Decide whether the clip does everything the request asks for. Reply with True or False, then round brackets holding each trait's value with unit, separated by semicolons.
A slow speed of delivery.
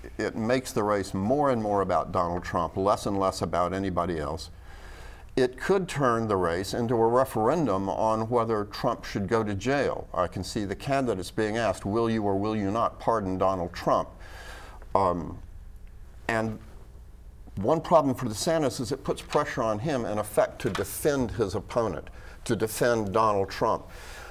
False (175 wpm)